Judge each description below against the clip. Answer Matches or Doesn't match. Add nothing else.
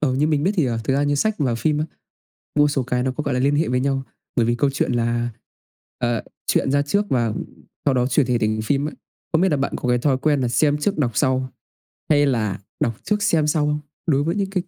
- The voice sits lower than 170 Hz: Matches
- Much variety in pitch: Doesn't match